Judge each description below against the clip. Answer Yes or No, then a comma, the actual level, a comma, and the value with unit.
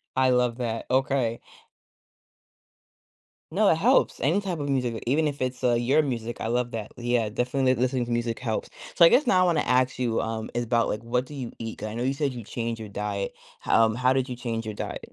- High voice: No, low, 125 Hz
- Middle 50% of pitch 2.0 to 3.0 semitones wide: Yes, narrow, 2.5 semitones